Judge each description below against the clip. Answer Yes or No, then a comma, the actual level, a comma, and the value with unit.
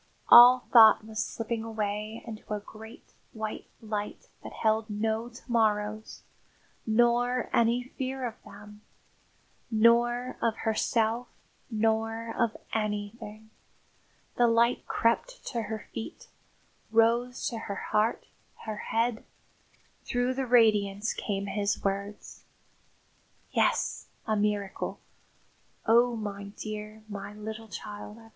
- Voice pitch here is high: Yes, high, 220 Hz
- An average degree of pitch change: No, narrow, 1.9 semitones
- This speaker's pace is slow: Yes, slow, 110 wpm